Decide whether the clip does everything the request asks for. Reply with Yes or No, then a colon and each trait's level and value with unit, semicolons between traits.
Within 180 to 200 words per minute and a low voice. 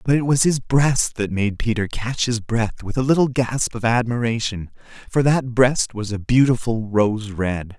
Yes: average, 195 wpm; low, 120 Hz